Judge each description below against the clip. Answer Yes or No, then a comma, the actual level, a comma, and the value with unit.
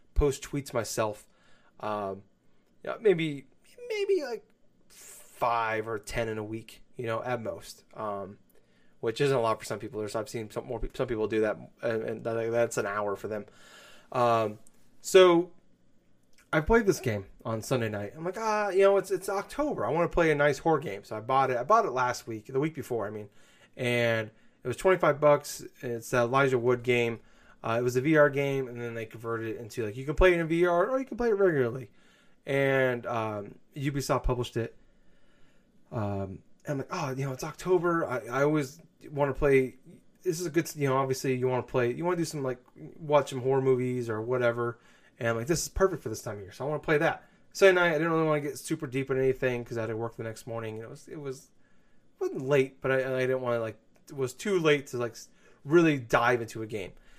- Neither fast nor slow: No, fast, 235 wpm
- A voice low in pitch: Yes, low, 130 Hz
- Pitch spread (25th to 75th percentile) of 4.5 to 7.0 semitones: Yes, average, 5.0 semitones